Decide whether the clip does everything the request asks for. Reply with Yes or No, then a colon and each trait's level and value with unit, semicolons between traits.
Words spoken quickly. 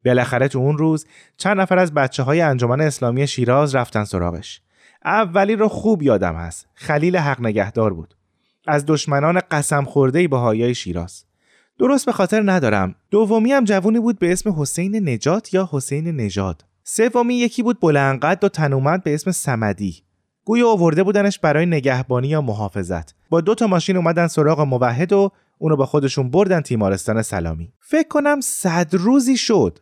Yes: fast, 160 wpm